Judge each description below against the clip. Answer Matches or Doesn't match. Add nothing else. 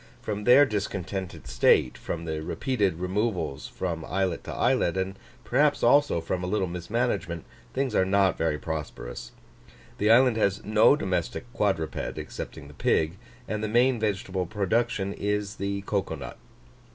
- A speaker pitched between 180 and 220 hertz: Doesn't match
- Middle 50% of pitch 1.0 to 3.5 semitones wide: Doesn't match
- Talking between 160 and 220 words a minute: Doesn't match